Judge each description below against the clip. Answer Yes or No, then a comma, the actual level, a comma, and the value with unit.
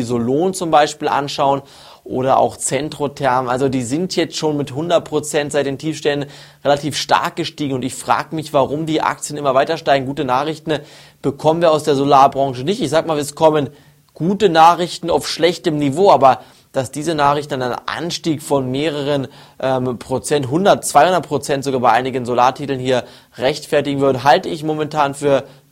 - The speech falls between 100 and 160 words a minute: No, average, 170 wpm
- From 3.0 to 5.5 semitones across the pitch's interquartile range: No, narrow, 2.4 semitones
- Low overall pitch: No, medium, 145 Hz